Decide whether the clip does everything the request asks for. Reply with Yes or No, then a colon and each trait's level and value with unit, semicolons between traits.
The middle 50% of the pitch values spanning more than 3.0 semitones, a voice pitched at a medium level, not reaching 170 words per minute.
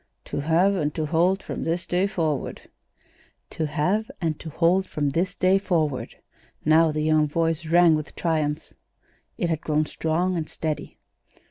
No: narrow, 2.5 semitones; medium, 165 Hz; average, 160 wpm